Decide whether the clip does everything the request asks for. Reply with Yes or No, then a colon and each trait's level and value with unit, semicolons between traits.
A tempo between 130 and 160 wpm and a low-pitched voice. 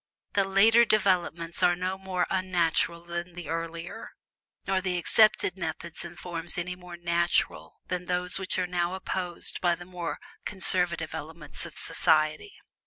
No: average, 150 wpm; medium, 175 Hz